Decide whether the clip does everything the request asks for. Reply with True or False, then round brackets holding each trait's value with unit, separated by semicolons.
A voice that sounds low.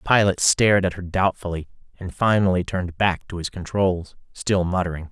True (90 Hz)